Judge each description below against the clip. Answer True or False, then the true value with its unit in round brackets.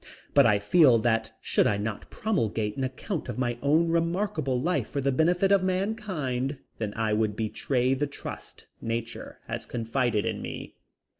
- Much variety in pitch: True (6.8 semitones)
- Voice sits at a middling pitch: False (130 Hz)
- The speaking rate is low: False (165 wpm)